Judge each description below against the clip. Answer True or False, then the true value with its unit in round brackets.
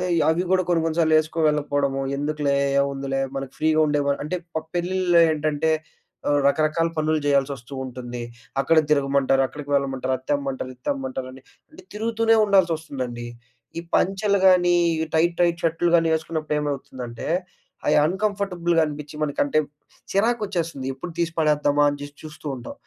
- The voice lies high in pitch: False (150 Hz)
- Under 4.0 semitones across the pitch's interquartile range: True (3.5 semitones)